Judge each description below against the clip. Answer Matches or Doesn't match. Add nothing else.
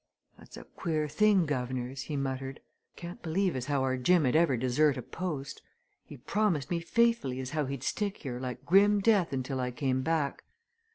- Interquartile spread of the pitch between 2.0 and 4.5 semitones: Doesn't match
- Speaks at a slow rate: Doesn't match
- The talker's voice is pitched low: Doesn't match